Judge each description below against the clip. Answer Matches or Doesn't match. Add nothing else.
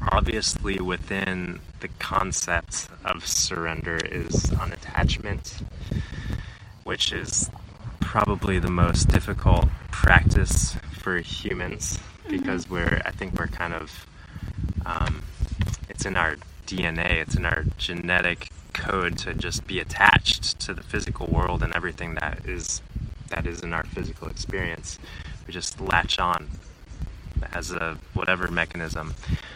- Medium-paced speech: Doesn't match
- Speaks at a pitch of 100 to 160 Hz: Doesn't match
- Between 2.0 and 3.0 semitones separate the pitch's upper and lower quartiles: Matches